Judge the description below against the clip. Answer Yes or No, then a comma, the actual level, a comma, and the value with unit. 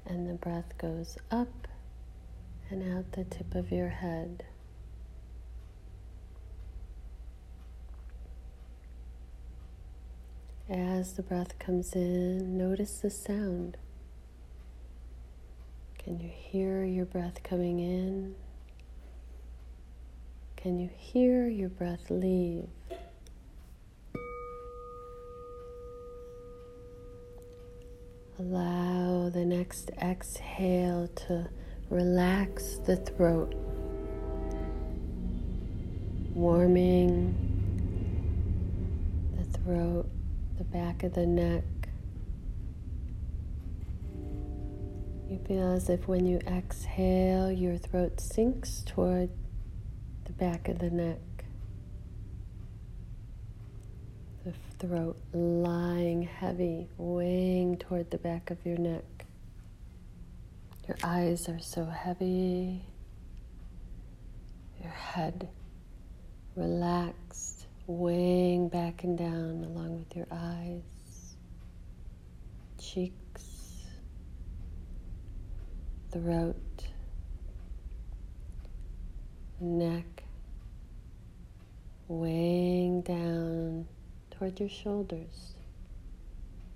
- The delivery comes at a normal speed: No, slow, 70 wpm